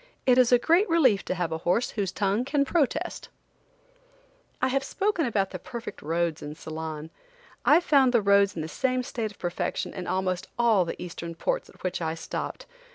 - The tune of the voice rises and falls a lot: Yes, wide, 6.9 semitones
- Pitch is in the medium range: No, high, 200 Hz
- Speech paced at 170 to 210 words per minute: Yes, average, 195 wpm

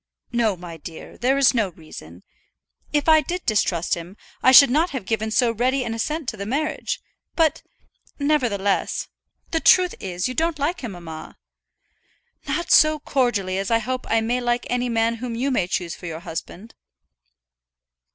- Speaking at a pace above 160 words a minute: Yes, average, 175 wpm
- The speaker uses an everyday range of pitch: No, wide, 6.3 semitones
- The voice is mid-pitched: No, high, 235 Hz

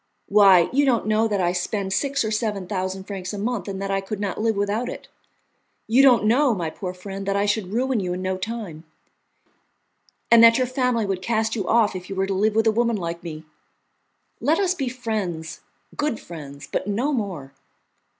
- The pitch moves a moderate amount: Yes, average, 3.7 semitones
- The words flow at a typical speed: No, fast, 210 wpm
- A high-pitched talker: Yes, high, 205 Hz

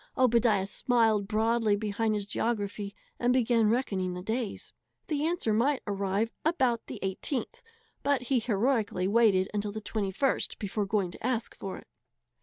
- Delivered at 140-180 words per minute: Yes, average, 150 wpm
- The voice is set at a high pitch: Yes, high, 220 Hz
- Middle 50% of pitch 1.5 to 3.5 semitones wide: Yes, average, 3.2 semitones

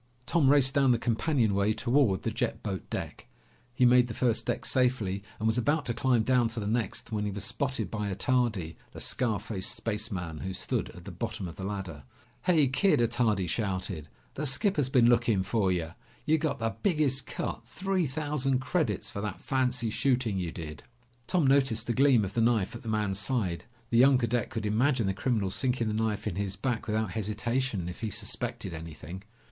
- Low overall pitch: Yes, low, 115 Hz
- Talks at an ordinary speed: Yes, average, 195 wpm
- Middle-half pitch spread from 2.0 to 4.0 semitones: No, average, 4.5 semitones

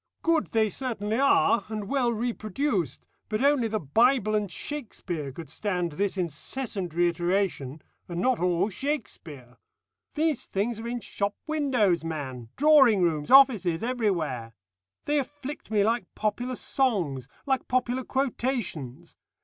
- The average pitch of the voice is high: Yes, high, 215 Hz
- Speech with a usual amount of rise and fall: No, wide, 6.8 semitones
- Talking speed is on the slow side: Yes, slow, 130 wpm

